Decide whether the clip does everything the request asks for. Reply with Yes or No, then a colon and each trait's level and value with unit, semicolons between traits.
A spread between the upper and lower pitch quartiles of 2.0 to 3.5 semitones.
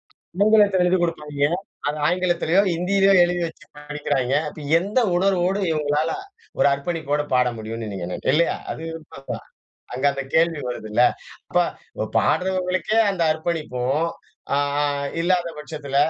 No: average, 4.1 semitones